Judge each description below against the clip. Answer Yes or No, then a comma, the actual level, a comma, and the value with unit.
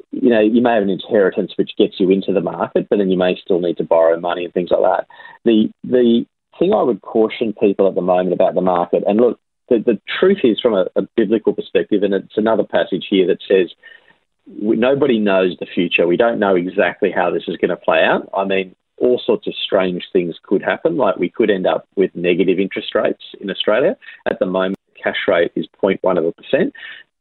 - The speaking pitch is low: Yes, low, 100 Hz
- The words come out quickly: Yes, fast, 225 wpm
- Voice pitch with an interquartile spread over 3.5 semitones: Yes, average, 4.4 semitones